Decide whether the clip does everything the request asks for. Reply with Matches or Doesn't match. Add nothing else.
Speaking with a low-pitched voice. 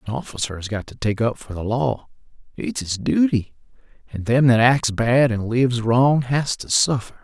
Matches